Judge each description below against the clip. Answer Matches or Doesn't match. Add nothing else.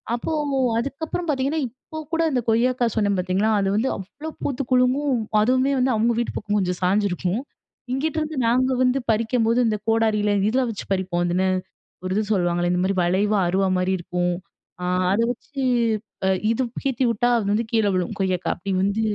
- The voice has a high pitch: Matches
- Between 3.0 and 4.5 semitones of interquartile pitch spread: Doesn't match